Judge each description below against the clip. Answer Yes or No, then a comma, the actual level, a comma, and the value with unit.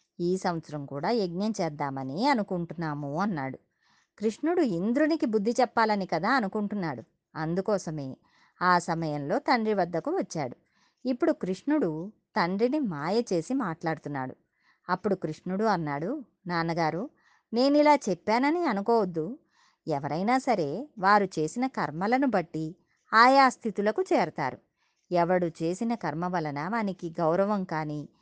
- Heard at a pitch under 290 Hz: Yes, high, 190 Hz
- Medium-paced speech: Yes, average, 100 wpm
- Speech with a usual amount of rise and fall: No, wide, 6.3 semitones